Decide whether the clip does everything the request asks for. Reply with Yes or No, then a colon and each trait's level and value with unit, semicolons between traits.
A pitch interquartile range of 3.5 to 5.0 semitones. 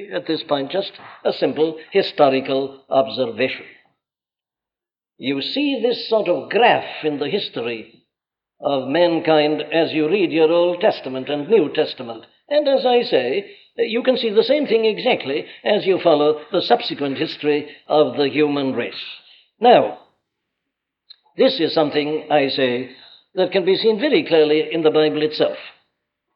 No: wide, 5.6 semitones